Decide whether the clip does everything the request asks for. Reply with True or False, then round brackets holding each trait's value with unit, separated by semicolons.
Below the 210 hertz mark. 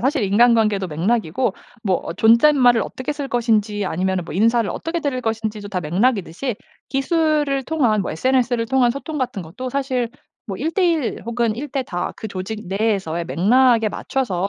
False (230 Hz)